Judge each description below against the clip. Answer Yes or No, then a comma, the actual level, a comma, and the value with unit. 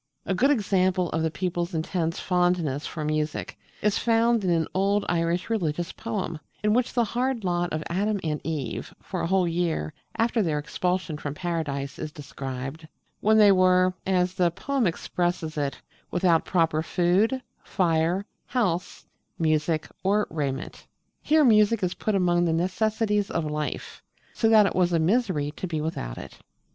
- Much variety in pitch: No, average, 4.1 semitones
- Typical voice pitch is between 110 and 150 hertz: No, medium, 175 Hz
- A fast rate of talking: No, average, 165 wpm